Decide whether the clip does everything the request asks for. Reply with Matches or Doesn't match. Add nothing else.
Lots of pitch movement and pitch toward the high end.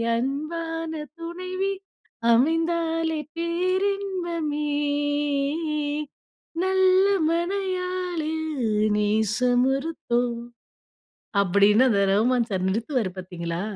Matches